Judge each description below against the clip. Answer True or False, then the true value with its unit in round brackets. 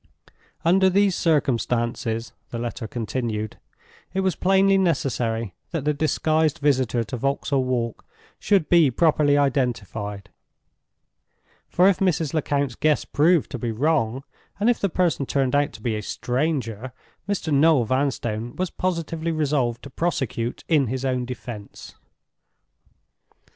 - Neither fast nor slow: False (130 wpm)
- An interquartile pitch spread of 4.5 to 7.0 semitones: True (5.3 semitones)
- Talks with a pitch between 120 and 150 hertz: True (140 Hz)